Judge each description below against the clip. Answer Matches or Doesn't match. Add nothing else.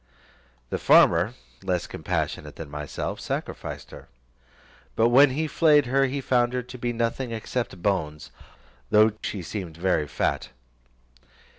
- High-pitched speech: Doesn't match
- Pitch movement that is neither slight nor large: Doesn't match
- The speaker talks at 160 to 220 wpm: Doesn't match